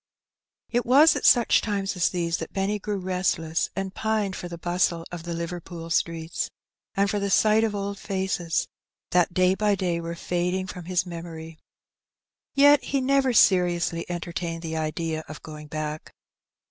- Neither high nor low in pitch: Yes, medium, 180 Hz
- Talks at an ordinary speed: Yes, average, 160 wpm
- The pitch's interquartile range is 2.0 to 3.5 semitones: Yes, average, 3.1 semitones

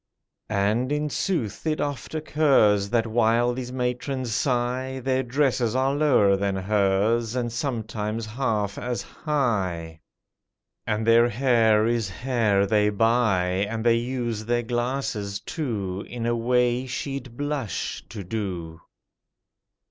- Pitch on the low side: Yes, low, 115 Hz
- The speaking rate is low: Yes, slow, 125 wpm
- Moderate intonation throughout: Yes, average, 3.5 semitones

